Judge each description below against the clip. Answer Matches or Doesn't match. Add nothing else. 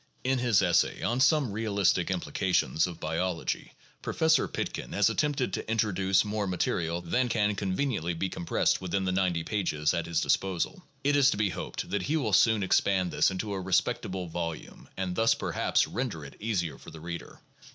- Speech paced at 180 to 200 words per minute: Matches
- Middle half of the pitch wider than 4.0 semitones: Matches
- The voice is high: Doesn't match